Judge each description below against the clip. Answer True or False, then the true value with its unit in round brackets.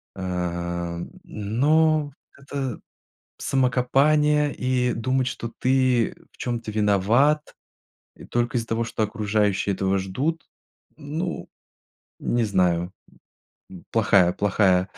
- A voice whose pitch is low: True (115 Hz)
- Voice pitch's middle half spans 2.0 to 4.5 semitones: False (5.5 semitones)